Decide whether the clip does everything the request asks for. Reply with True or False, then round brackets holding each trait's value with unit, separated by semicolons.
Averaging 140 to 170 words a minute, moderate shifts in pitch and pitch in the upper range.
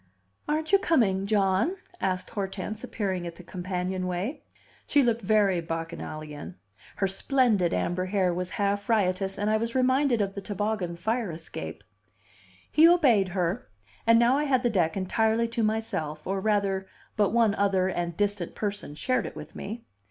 True (160 wpm; 3.8 semitones; 200 Hz)